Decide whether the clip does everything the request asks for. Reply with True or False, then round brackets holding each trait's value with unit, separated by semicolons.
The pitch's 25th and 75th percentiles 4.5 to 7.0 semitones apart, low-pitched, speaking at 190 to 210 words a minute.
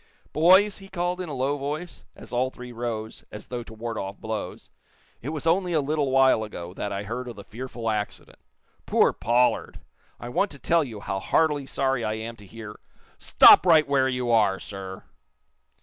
True (5.2 semitones; 125 Hz; 195 wpm)